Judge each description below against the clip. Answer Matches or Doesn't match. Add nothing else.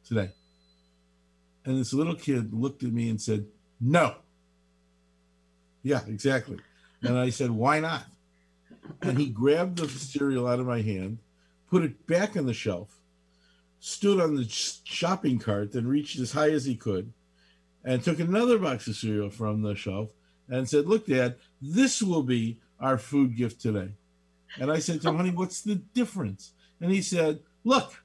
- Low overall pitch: Matches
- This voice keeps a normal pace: Matches